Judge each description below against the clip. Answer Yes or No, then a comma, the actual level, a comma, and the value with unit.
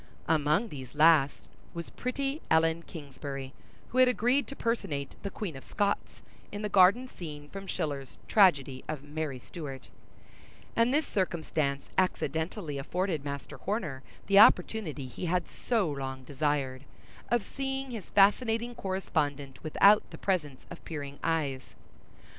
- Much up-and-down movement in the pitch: Yes, wide, 6.4 semitones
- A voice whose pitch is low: No, medium, 165 Hz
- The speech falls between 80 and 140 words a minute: Yes, slow, 135 wpm